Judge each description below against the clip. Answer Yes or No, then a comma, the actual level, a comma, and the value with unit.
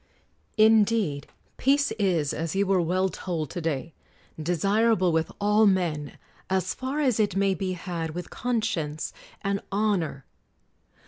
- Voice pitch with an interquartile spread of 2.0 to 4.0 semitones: No, average, 4.5 semitones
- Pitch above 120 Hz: Yes, high, 190 Hz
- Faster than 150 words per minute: No, slow, 135 wpm